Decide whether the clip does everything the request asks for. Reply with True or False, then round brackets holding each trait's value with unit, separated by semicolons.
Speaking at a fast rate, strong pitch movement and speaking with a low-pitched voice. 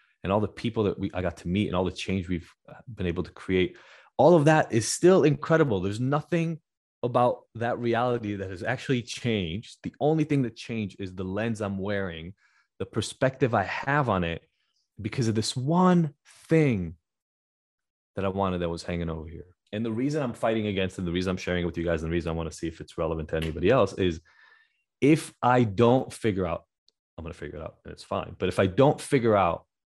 True (225 wpm; 6.7 semitones; 105 Hz)